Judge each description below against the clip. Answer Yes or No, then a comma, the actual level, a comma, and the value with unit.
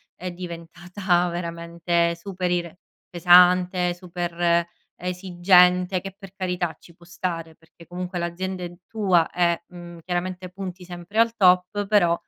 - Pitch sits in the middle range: Yes, medium, 180 Hz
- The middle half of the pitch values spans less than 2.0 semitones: Yes, narrow, 1.1 semitones